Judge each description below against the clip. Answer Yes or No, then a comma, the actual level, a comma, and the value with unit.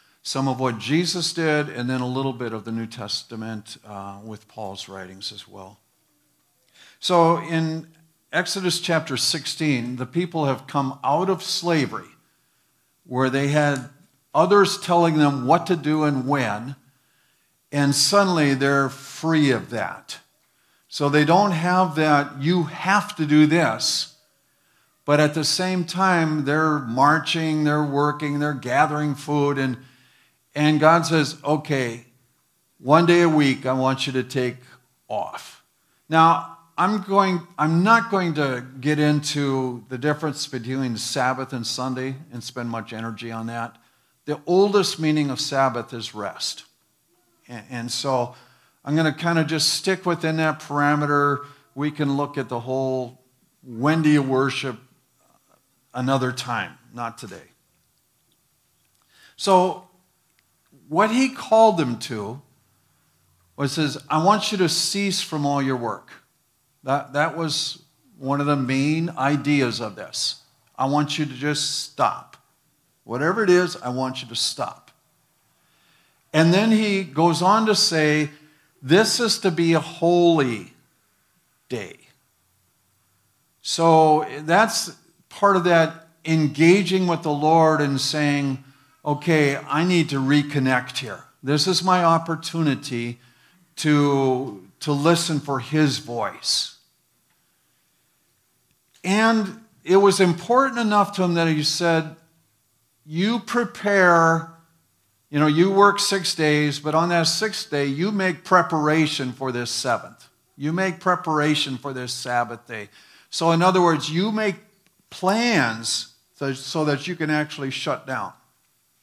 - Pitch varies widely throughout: No, average, 4.3 semitones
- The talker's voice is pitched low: No, medium, 150 Hz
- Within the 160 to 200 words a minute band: No, average, 140 wpm